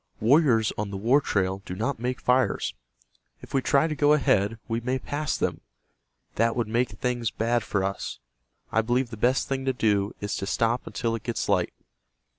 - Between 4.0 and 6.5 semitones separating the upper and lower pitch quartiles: No, average, 3.4 semitones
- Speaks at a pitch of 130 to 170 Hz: No, low, 115 Hz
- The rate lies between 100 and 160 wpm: No, average, 195 wpm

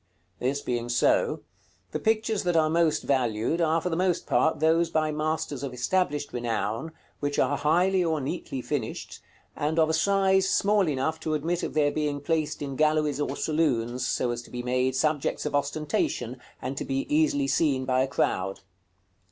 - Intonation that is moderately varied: Yes, average, 3.7 semitones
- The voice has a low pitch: No, medium, 150 Hz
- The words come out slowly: No, average, 185 wpm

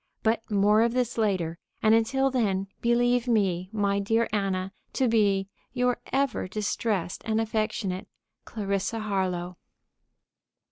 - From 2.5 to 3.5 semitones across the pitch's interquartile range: Yes, average, 3.1 semitones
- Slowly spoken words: Yes, slow, 125 wpm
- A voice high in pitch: Yes, high, 215 Hz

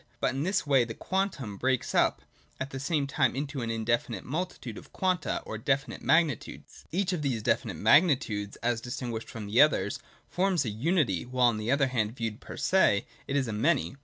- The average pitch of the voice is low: Yes, low, 130 Hz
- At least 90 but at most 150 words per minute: No, average, 195 wpm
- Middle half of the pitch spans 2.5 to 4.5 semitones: No, average, 4.9 semitones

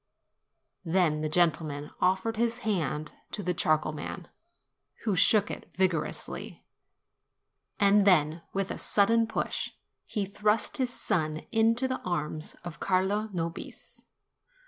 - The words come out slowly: Yes, slow, 125 wpm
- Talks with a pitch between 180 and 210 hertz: Yes, medium, 185 Hz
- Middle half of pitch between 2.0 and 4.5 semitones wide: No, average, 5.2 semitones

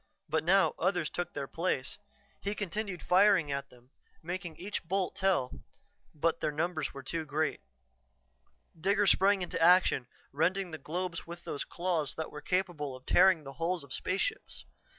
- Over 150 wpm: Yes, average, 160 wpm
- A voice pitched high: No, medium, 170 Hz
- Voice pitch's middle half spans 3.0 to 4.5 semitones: Yes, average, 3.7 semitones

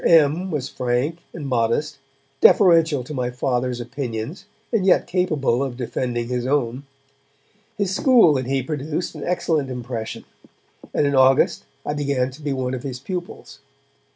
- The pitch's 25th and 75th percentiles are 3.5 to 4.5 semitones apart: Yes, average, 4.0 semitones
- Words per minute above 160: No, average, 155 wpm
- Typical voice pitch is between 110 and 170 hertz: Yes, low, 135 Hz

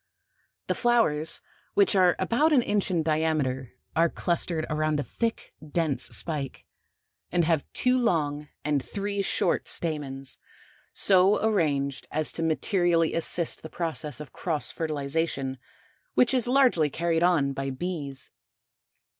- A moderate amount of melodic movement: Yes, average, 4.0 semitones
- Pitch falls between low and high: Yes, medium, 160 Hz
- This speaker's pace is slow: Yes, slow, 130 wpm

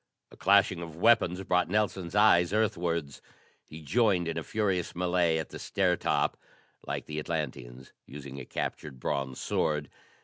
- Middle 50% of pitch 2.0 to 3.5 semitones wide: No, average, 4.0 semitones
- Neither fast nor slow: Yes, average, 150 wpm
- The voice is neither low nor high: No, very low, 85 Hz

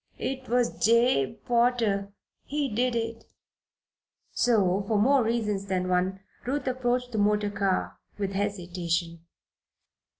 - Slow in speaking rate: Yes, slow, 120 wpm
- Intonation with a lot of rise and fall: No, average, 4.1 semitones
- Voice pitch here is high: Yes, high, 210 Hz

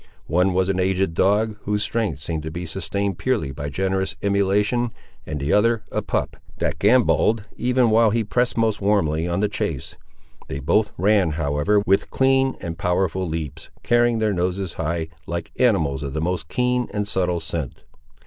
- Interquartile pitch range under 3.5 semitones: No, average, 4.7 semitones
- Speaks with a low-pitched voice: Yes, very low, 95 Hz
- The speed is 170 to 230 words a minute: Yes, average, 175 wpm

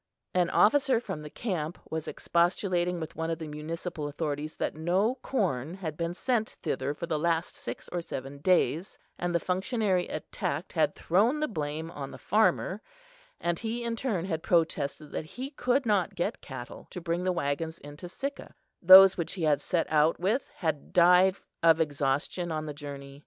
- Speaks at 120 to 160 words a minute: No, average, 180 wpm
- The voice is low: No, medium, 170 Hz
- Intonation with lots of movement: No, average, 3.7 semitones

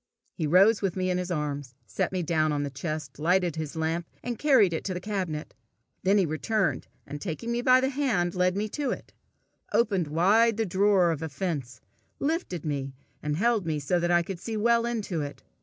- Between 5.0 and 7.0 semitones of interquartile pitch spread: Yes, wide, 5.4 semitones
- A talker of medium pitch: Yes, medium, 180 Hz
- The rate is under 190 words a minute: No, fast, 205 wpm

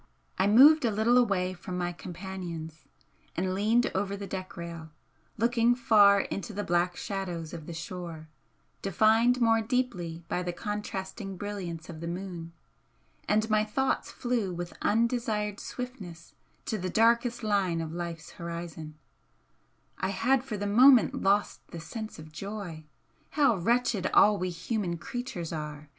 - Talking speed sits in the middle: Yes, average, 150 wpm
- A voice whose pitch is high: Yes, high, 195 Hz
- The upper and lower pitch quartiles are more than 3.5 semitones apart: Yes, average, 4.6 semitones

